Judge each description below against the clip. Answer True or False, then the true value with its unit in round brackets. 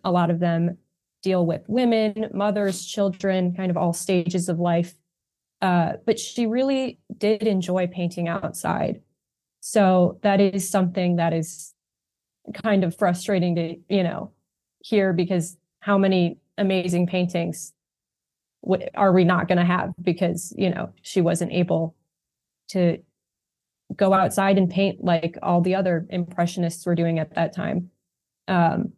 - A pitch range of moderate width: False (2.2 semitones)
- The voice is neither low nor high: True (180 Hz)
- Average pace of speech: True (145 wpm)